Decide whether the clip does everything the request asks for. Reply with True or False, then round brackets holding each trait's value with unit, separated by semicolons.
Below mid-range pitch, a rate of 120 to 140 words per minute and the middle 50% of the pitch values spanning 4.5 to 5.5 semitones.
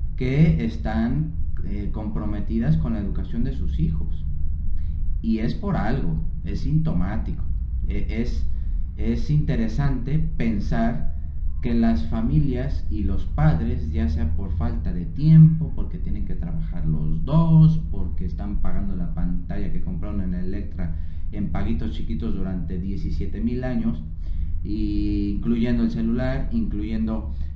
True (80 Hz; 130 wpm; 4.8 semitones)